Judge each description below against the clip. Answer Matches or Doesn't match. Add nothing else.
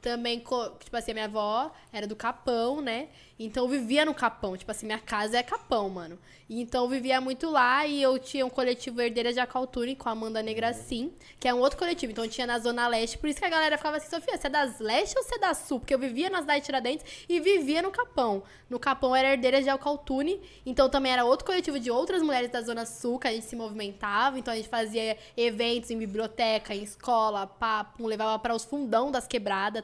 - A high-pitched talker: Matches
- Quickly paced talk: Matches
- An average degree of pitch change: Matches